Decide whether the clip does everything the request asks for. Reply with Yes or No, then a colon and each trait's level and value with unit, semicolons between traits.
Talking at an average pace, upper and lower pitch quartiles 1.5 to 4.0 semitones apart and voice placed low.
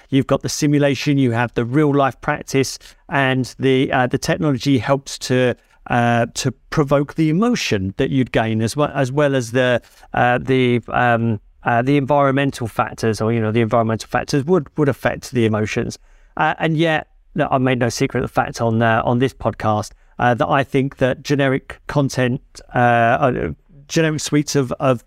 Yes: average, 185 wpm; average, 3.3 semitones; low, 130 Hz